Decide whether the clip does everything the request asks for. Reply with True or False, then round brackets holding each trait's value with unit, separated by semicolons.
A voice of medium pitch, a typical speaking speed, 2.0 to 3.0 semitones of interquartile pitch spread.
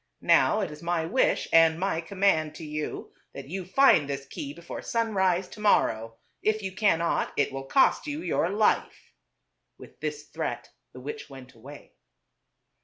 False (165 Hz; 165 wpm; 5.3 semitones)